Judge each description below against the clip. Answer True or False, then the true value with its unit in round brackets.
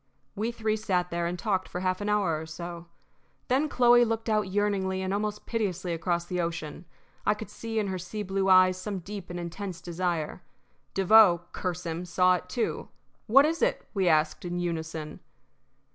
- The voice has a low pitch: False (185 Hz)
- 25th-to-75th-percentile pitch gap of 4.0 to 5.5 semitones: False (3.3 semitones)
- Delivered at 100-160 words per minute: False (185 wpm)